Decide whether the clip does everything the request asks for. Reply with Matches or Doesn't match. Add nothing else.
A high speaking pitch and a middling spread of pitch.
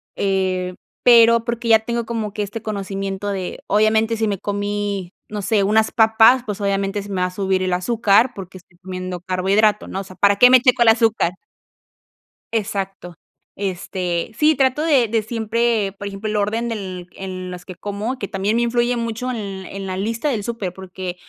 Matches